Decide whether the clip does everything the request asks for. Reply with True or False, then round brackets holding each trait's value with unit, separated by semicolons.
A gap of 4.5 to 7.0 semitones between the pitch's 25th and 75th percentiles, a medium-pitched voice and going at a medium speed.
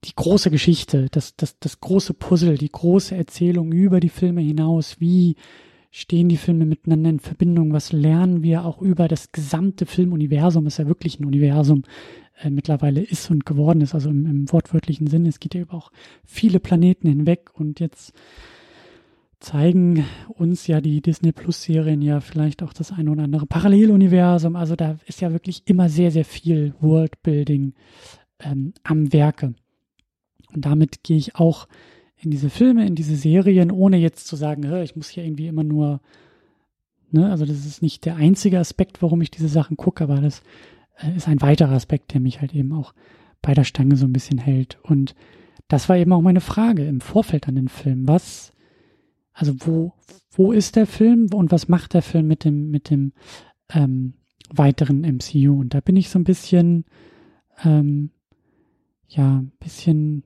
False (2.9 semitones; 160 Hz; 175 wpm)